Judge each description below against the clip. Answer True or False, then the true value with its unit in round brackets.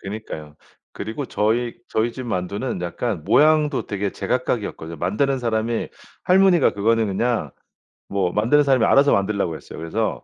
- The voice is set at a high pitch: False (110 Hz)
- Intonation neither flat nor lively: True (4.7 semitones)